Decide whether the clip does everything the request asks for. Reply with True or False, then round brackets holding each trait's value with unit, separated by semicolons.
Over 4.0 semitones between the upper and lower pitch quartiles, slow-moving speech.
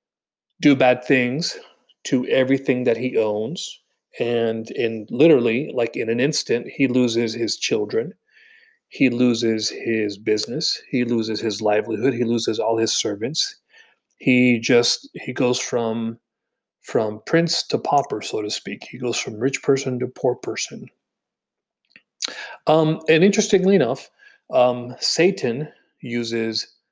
True (5.4 semitones; 130 wpm)